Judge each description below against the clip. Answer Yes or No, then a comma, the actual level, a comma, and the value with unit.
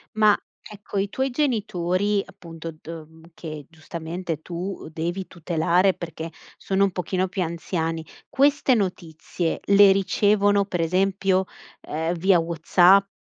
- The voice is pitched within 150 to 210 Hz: Yes, medium, 185 Hz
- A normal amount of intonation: Yes, average, 3.1 semitones